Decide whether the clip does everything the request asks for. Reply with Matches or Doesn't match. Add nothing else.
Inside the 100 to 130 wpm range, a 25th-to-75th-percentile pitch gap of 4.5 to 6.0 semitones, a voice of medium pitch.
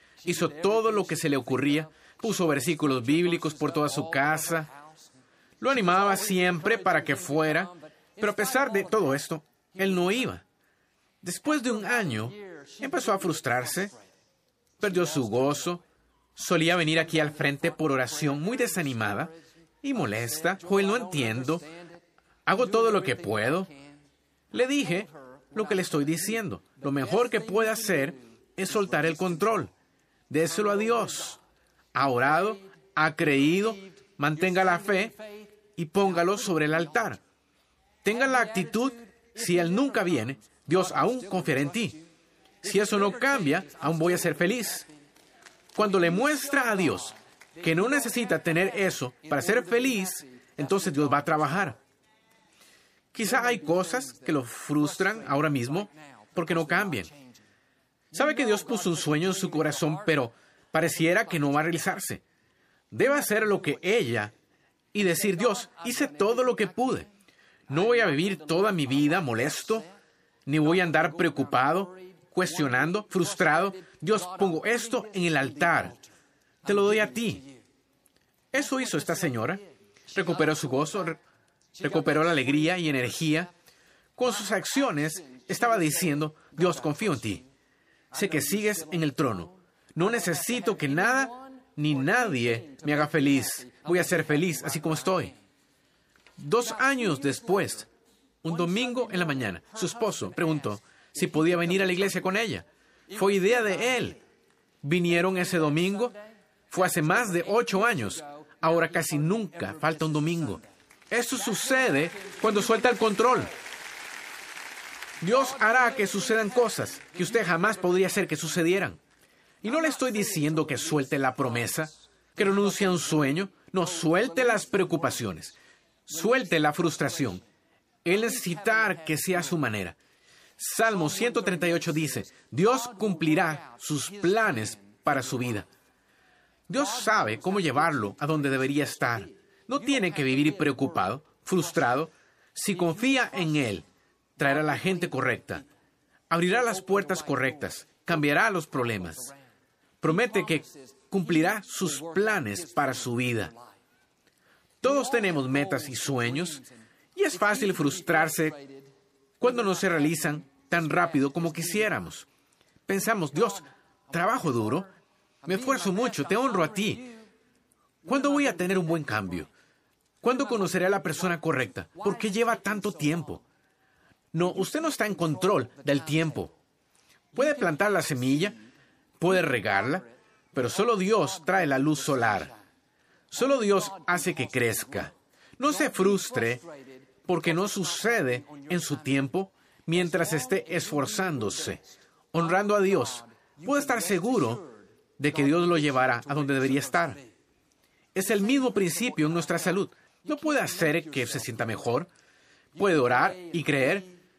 Doesn't match